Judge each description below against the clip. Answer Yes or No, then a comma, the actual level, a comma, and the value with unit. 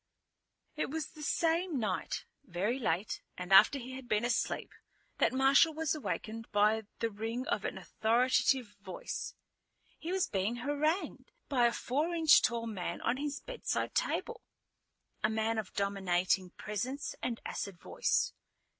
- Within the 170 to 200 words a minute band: No, average, 145 wpm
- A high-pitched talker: Yes, high, 235 Hz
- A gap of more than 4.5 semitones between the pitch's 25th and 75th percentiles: Yes, wide, 5.6 semitones